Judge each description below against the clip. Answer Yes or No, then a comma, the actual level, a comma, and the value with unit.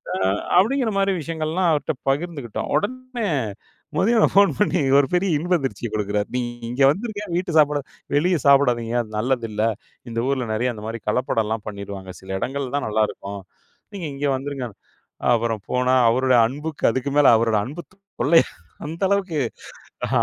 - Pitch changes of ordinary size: No, wide, 7.0 semitones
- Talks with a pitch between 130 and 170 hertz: Yes, medium, 140 Hz